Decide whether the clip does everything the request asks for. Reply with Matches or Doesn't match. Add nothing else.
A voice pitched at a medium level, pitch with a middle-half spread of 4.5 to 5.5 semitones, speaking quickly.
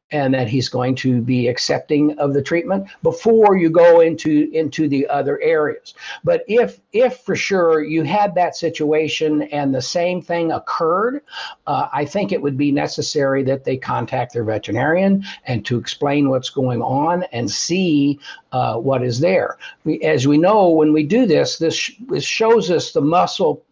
Doesn't match